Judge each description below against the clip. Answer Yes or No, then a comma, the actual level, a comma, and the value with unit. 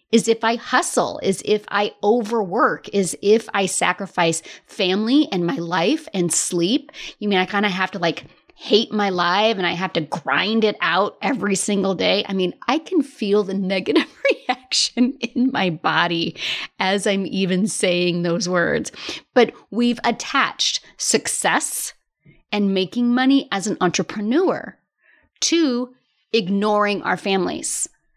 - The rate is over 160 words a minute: No, average, 150 wpm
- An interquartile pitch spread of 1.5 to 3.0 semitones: No, average, 4.2 semitones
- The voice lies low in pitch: No, high, 205 Hz